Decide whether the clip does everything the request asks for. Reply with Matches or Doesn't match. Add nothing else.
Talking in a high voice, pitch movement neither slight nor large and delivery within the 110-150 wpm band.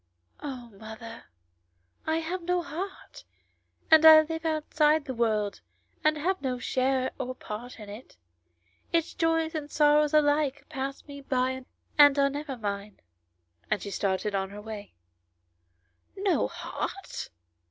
Doesn't match